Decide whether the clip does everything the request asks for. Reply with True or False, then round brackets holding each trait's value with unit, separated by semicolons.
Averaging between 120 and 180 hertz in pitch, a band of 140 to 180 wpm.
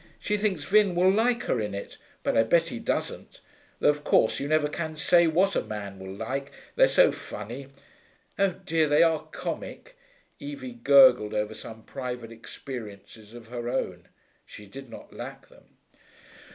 True (140 Hz; 170 wpm)